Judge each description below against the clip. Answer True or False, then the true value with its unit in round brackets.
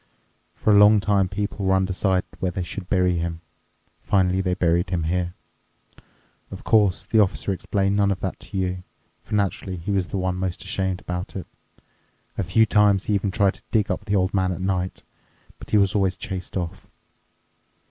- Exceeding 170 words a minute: True (190 wpm)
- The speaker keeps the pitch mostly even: True (1.8 semitones)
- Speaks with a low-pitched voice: True (95 Hz)